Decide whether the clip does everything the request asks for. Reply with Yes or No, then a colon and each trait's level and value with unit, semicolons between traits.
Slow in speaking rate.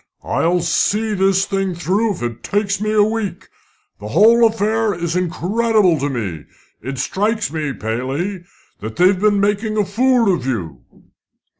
No: average, 155 wpm